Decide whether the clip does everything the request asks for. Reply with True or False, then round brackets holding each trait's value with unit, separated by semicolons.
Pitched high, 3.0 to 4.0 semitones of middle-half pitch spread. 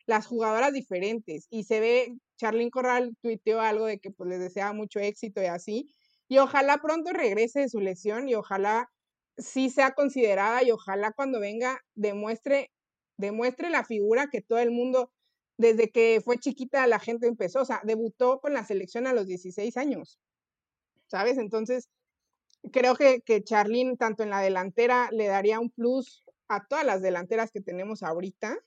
True (230 Hz; 3.3 semitones)